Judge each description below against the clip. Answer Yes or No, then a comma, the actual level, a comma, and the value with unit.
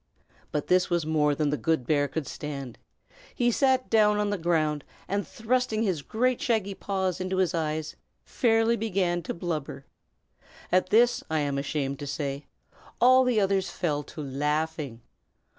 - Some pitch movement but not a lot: No, wide, 6.0 semitones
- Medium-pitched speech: Yes, medium, 175 Hz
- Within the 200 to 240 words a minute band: No, average, 160 wpm